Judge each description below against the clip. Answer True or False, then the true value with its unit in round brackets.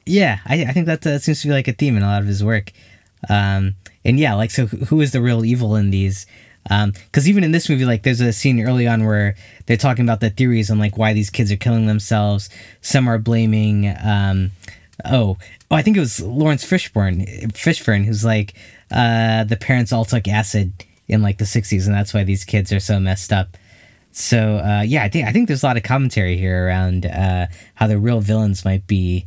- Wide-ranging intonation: False (3.3 semitones)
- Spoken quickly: True (230 wpm)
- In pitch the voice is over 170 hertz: False (110 Hz)